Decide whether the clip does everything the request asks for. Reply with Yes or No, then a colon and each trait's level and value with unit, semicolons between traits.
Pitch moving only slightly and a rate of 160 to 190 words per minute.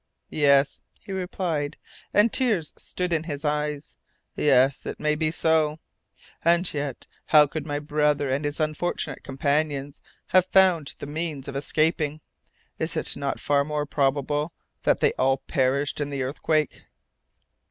No: narrow, 2.1 semitones; average, 145 wpm